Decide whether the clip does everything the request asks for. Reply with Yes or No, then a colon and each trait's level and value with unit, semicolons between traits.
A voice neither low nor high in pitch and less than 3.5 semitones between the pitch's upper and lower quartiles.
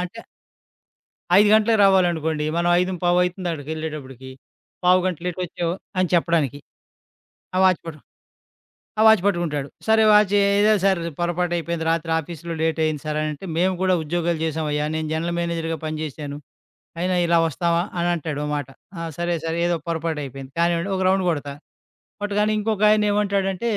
Yes: medium, 170 Hz; average, 2.9 semitones